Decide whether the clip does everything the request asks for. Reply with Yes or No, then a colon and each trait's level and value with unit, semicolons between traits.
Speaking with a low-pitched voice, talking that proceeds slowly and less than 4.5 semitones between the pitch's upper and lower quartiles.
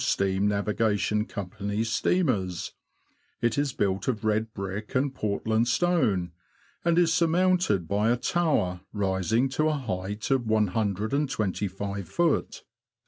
No: low, 110 Hz; slow, 120 wpm; average, 5.3 semitones